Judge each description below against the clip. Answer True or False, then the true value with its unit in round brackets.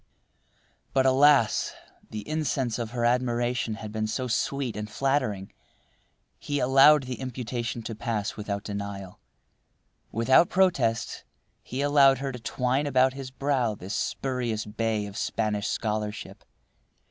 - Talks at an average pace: False (130 wpm)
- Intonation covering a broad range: False (3.7 semitones)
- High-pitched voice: False (120 Hz)